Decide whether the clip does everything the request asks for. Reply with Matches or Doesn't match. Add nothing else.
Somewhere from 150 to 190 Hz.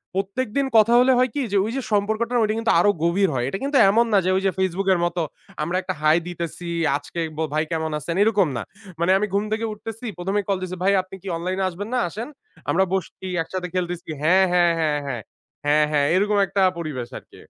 Matches